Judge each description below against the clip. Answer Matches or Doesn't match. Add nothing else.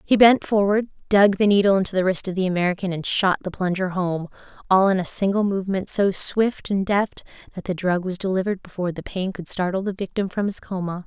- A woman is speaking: Matches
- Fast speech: Matches